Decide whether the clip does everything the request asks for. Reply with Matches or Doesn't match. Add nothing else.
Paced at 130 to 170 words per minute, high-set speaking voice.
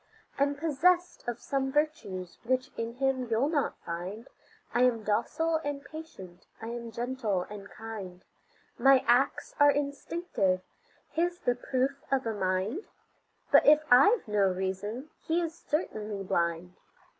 Matches